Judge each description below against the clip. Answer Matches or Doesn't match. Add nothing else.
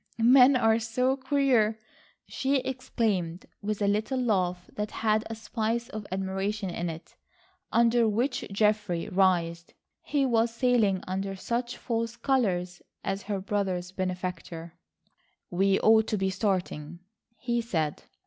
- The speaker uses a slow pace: Matches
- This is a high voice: Matches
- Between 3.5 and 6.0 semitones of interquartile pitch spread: Matches